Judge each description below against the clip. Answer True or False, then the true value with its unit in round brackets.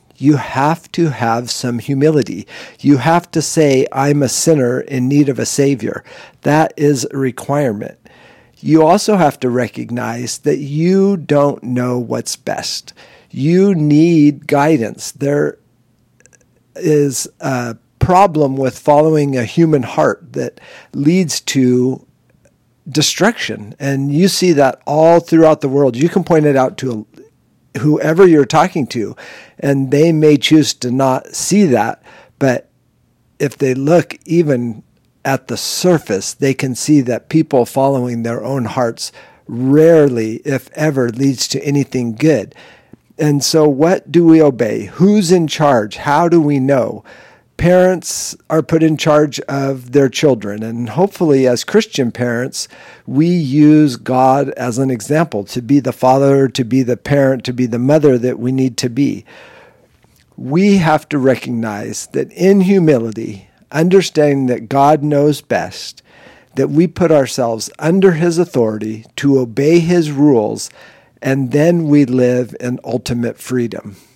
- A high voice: False (140 Hz)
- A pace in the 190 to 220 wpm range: False (145 wpm)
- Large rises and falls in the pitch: False (3.9 semitones)